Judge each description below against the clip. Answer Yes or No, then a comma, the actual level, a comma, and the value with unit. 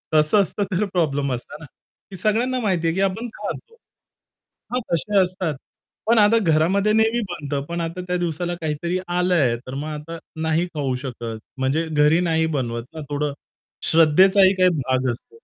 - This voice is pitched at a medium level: Yes, medium, 165 Hz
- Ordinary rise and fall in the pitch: Yes, average, 4.3 semitones